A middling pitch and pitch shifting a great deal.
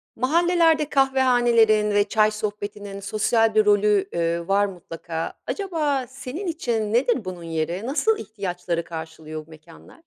No: high, 210 Hz; wide, 6.6 semitones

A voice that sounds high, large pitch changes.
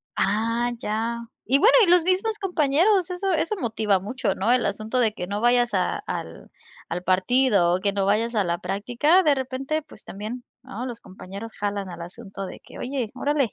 Yes: high, 235 Hz; wide, 5.7 semitones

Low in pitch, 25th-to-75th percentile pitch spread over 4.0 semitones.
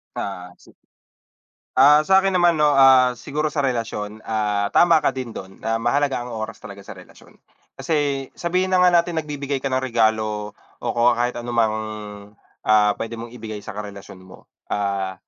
Yes: low, 120 Hz; wide, 5.4 semitones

